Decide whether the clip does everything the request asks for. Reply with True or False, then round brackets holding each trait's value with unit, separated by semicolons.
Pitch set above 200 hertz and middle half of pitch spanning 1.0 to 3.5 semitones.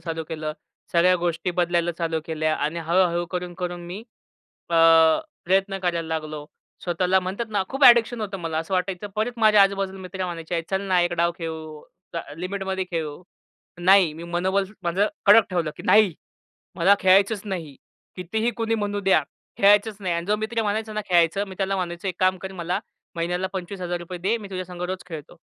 False (185 Hz; 2.6 semitones)